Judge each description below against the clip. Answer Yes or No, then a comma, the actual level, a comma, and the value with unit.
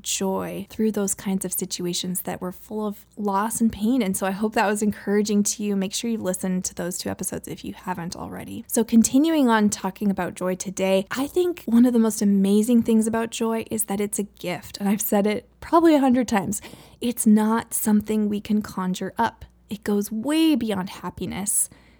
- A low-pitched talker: No, high, 210 Hz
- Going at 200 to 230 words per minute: Yes, fast, 205 wpm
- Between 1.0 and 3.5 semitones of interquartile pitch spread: Yes, average, 2.9 semitones